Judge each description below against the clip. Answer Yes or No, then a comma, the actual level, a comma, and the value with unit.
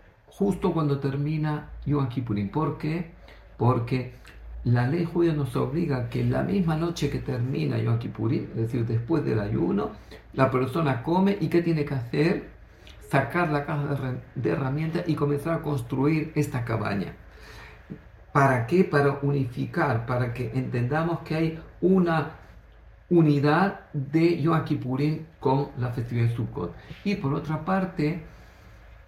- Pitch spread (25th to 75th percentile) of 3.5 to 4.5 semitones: Yes, average, 4.2 semitones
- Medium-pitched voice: Yes, medium, 145 Hz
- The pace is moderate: Yes, average, 140 wpm